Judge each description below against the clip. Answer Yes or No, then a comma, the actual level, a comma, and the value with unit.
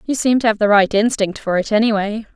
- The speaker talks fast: Yes, fast, 255 wpm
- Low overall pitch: No, high, 215 Hz